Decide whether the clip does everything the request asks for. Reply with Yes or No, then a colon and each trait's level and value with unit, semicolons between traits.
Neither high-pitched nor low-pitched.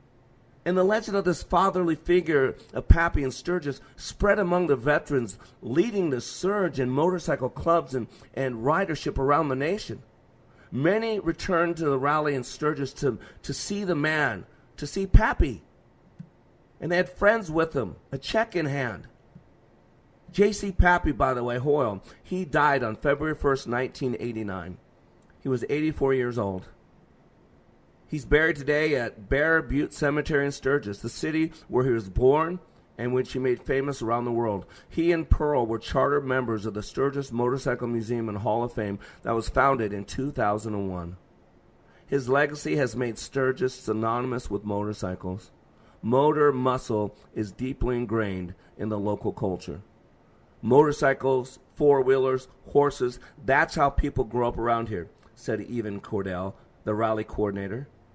No: low, 130 Hz